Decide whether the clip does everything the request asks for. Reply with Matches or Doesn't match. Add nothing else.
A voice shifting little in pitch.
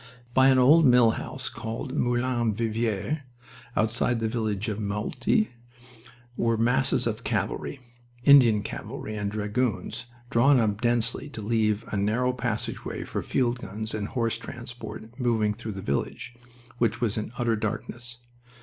Matches